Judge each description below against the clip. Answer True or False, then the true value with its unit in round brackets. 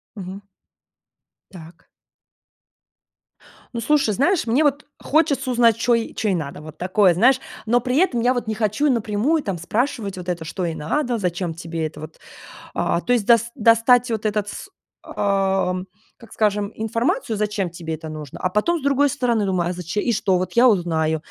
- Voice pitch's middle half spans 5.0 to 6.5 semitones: True (5.4 semitones)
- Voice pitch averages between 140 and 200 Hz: False (210 Hz)